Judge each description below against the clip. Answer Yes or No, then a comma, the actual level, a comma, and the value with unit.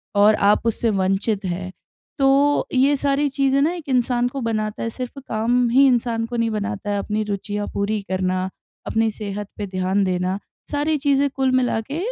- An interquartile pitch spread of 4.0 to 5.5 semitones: Yes, average, 4.8 semitones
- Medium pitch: No, high, 225 Hz